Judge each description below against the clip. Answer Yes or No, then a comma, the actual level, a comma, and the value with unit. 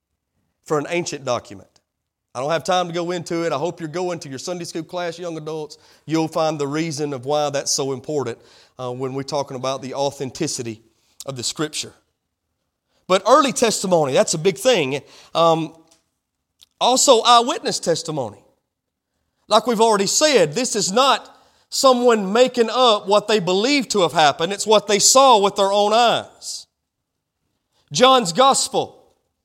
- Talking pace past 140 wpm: Yes, average, 160 wpm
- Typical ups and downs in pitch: No, wide, 7.7 semitones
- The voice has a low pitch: No, medium, 170 Hz